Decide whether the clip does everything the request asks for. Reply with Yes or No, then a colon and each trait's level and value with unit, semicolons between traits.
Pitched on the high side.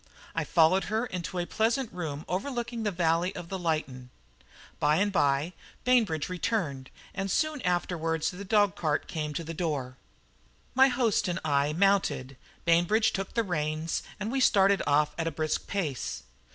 No: medium, 175 Hz